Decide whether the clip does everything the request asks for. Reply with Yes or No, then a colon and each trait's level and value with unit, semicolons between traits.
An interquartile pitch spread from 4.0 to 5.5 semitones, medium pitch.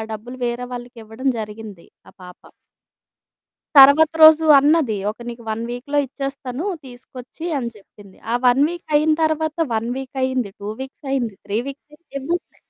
No: average, 4.4 semitones; very high, 255 Hz